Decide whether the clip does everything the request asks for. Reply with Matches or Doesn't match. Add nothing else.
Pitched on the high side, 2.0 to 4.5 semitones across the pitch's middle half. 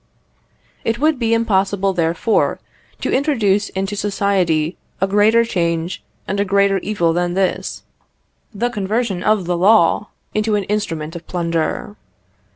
Matches